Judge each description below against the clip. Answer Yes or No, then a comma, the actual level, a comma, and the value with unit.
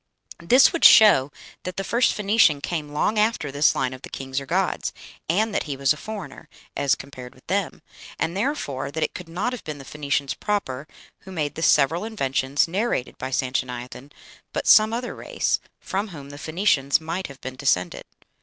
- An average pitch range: No, wide, 6.7 semitones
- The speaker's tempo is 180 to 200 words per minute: Yes, average, 190 wpm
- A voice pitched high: No, medium, 150 Hz